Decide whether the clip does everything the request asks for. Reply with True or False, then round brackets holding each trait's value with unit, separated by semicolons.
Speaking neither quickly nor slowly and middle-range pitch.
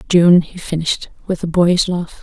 True (190 wpm; 170 Hz)